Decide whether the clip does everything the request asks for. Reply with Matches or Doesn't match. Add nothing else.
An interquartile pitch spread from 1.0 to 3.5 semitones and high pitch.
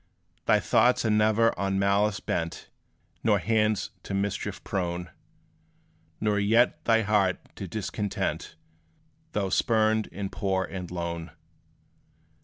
Doesn't match